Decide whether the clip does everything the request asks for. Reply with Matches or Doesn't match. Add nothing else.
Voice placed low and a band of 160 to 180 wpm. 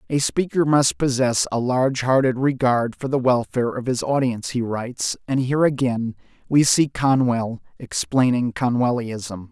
Doesn't match